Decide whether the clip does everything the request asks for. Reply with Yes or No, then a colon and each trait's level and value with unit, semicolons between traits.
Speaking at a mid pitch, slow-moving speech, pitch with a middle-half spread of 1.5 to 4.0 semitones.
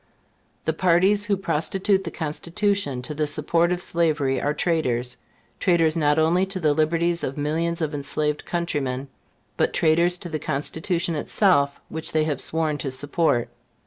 No: medium, 160 Hz; average, 155 wpm; average, 2.8 semitones